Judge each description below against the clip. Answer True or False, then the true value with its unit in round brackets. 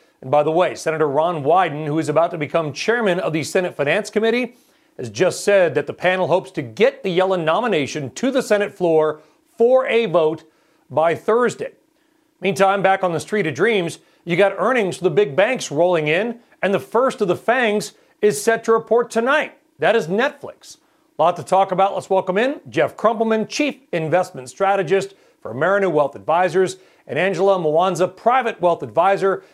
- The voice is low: False (190 Hz)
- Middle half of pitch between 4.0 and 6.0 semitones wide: True (5.2 semitones)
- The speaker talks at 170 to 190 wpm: True (185 wpm)